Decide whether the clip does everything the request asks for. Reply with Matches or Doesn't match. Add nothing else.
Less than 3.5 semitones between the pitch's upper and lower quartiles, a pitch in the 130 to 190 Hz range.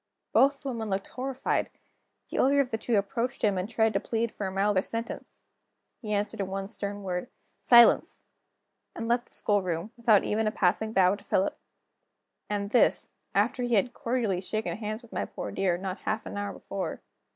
Doesn't match